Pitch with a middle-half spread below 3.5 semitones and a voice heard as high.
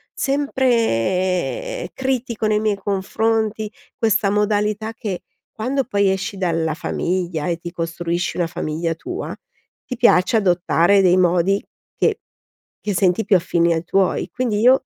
No: average, 4.3 semitones; high, 200 Hz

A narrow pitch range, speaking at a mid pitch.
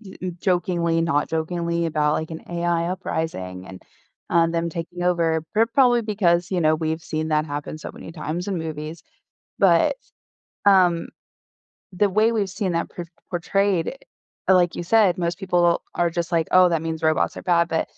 Yes: narrow, 2.2 semitones; medium, 170 Hz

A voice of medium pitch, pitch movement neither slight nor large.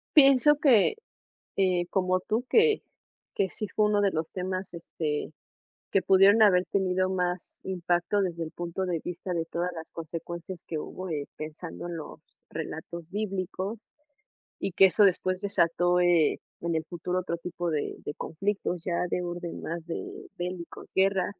No: medium, 180 Hz; narrow, 2.2 semitones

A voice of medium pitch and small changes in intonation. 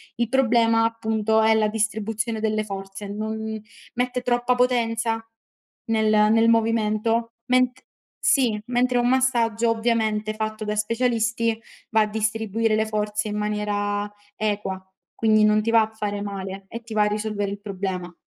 No: high, 220 Hz; narrow, 1.5 semitones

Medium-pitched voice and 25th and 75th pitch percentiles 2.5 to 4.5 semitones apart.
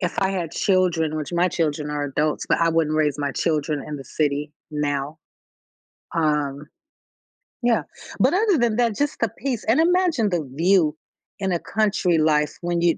No: medium, 165 Hz; average, 4.9 semitones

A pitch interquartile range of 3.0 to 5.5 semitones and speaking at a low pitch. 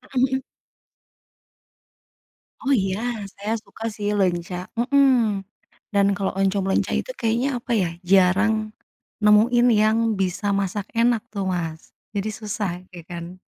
No: average, 3.4 semitones; high, 210 Hz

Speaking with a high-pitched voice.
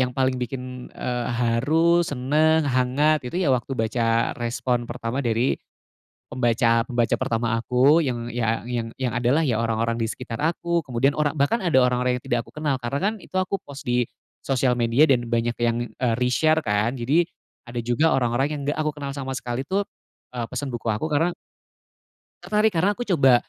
No: low, 125 Hz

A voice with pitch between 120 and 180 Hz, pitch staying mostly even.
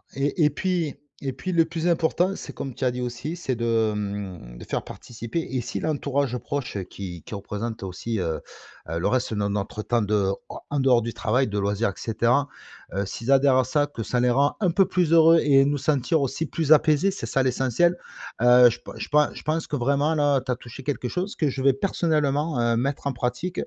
No: low, 135 Hz; average, 4.5 semitones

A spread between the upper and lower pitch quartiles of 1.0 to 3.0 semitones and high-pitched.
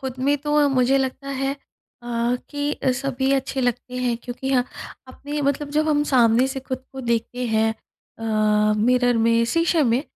Yes: average, 2.7 semitones; very high, 255 Hz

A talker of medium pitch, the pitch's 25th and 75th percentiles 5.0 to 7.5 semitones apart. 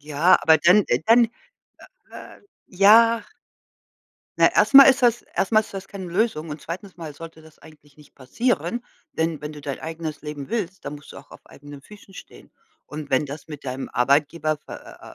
Yes: medium, 160 Hz; wide, 5.4 semitones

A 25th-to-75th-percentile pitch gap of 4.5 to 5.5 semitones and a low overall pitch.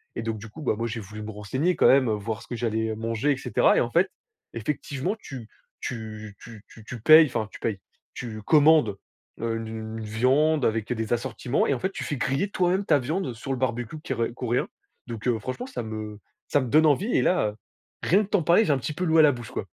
Yes: average, 5.2 semitones; low, 120 Hz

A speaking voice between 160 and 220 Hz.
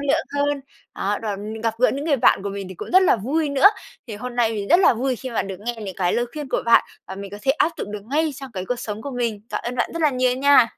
No: high, 240 Hz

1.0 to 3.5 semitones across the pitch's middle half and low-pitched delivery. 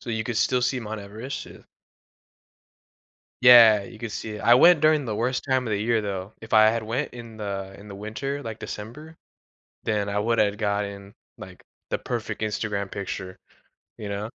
Yes: average, 2.9 semitones; low, 110 Hz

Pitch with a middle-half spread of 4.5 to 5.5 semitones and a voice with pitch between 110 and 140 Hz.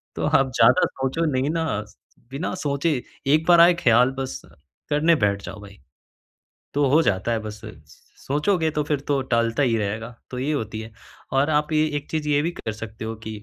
Yes: average, 5.2 semitones; low, 135 Hz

